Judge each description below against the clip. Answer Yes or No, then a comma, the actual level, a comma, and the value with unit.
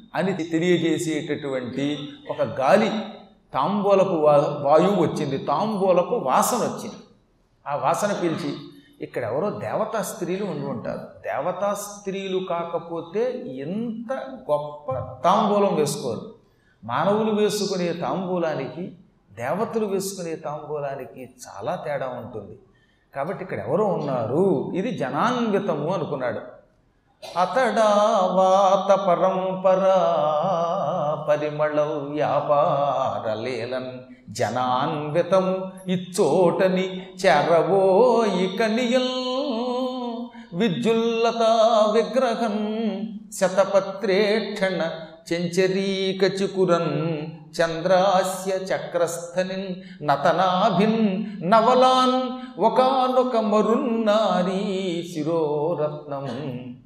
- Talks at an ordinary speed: No, slow, 65 wpm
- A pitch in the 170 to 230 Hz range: Yes, medium, 185 Hz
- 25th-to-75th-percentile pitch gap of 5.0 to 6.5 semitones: Yes, average, 5.3 semitones